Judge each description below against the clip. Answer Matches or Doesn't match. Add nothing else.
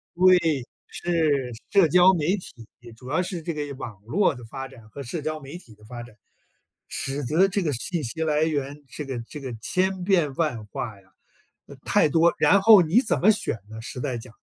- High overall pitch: Doesn't match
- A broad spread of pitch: Matches